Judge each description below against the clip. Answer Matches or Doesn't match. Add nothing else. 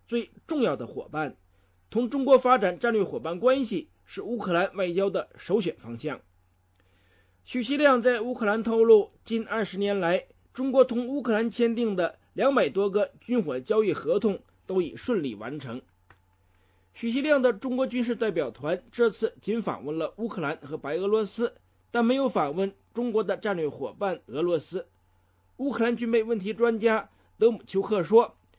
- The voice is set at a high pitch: Matches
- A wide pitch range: Matches